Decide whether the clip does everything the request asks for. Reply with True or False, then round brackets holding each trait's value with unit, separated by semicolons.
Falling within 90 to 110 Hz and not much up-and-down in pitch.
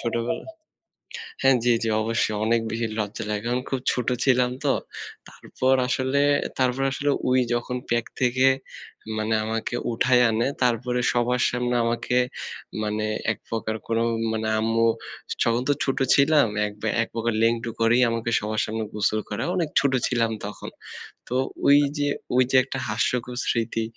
False (120 Hz; 2.1 semitones)